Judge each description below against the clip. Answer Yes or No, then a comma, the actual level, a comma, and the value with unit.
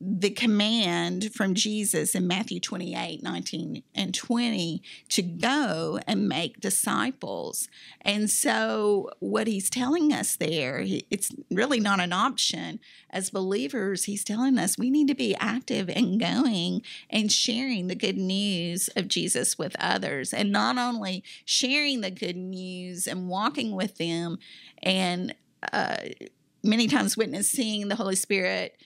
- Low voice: No, high, 205 Hz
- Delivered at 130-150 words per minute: Yes, average, 140 wpm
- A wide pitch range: No, average, 4.2 semitones